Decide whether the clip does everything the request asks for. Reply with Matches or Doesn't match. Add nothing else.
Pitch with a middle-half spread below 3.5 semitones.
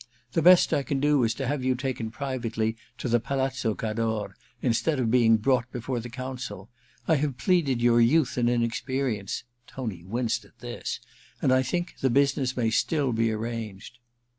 Matches